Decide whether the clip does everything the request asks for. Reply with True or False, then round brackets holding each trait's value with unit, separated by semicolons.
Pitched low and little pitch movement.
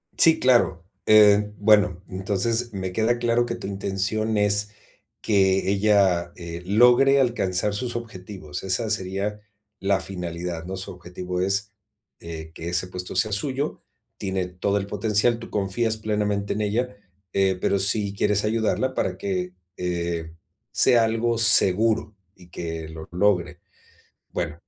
False (100 Hz; 3.2 semitones)